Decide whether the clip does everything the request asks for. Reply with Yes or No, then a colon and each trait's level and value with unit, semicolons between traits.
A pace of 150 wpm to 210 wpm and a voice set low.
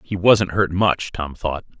Yes: average, 200 wpm; very low, 90 Hz